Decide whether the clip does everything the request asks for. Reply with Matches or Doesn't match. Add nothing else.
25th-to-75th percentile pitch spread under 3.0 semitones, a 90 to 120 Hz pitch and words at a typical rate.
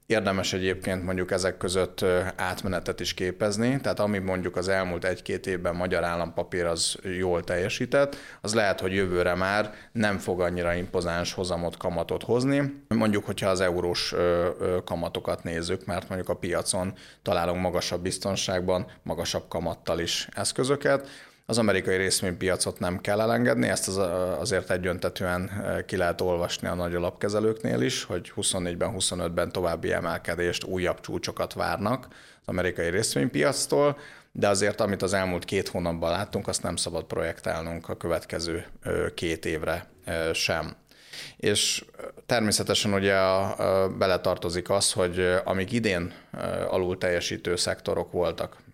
Matches